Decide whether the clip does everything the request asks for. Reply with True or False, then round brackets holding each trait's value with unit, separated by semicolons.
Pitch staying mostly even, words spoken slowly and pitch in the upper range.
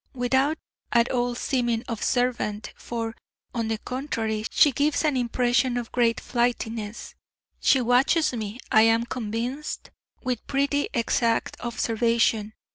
True (2.1 semitones; 120 wpm; 240 Hz)